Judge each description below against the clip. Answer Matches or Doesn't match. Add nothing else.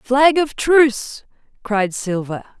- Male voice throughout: Doesn't match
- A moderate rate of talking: Doesn't match